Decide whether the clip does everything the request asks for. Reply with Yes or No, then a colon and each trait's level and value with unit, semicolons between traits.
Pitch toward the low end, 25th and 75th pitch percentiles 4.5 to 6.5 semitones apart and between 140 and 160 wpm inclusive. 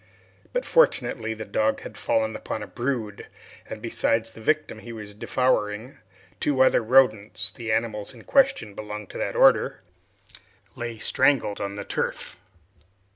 No: low, 110 Hz; average, 3.4 semitones; average, 145 wpm